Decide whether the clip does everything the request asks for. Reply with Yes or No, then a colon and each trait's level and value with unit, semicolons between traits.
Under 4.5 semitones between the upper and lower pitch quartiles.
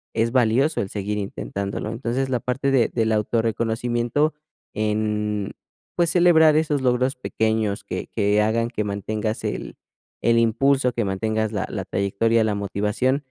Yes: average, 3.1 semitones